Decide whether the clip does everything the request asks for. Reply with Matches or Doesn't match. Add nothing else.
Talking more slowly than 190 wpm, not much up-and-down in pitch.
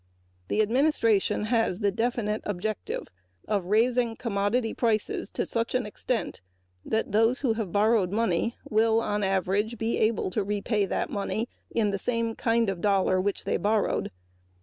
Matches